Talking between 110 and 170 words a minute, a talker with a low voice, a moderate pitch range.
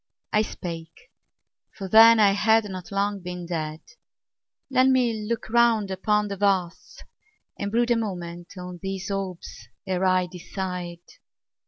No: average, 140 wpm; high, 195 Hz; average, 3.3 semitones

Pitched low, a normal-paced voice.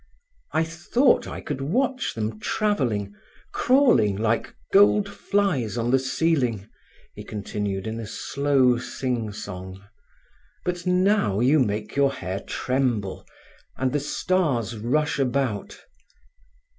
No: low, 130 Hz; slow, 120 wpm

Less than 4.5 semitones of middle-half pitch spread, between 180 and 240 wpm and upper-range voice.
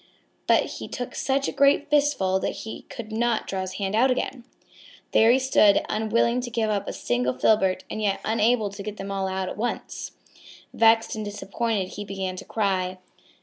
Yes: average, 3.4 semitones; average, 190 wpm; high, 215 Hz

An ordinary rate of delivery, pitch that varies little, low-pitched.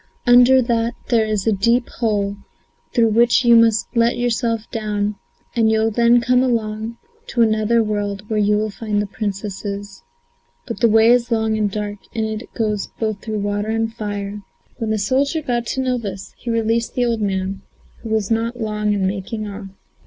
No: average, 180 wpm; narrow, 2.1 semitones; high, 220 Hz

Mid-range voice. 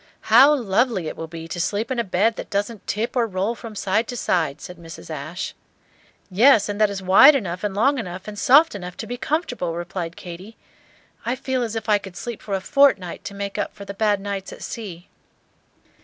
No: high, 200 Hz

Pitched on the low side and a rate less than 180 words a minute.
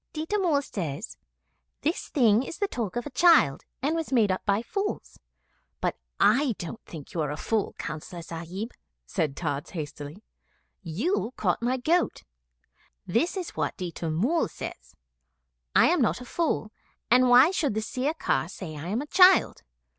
No: high, 225 Hz; average, 165 wpm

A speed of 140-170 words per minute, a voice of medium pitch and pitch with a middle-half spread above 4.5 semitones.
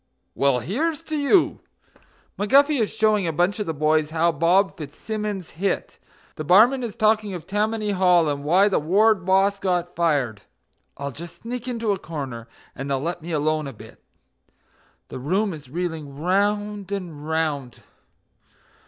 Yes: average, 160 wpm; medium, 180 Hz; average, 5.3 semitones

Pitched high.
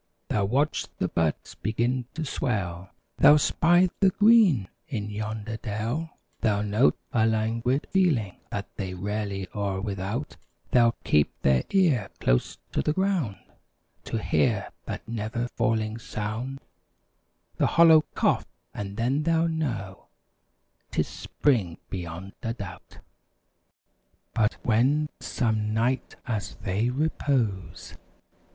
No: low, 115 Hz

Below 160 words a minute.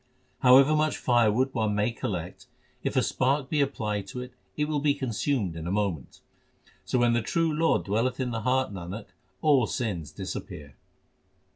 No: average, 170 wpm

